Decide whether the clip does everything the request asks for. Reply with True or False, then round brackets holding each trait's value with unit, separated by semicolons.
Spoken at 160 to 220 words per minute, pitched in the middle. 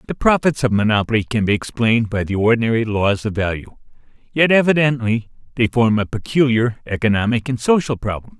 False (165 wpm; 115 Hz)